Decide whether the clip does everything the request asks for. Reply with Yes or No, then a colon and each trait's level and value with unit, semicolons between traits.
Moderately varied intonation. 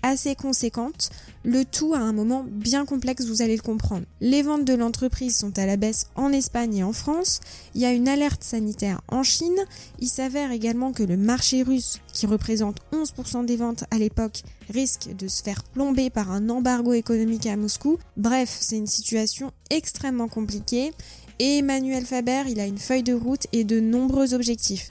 Yes: average, 3.1 semitones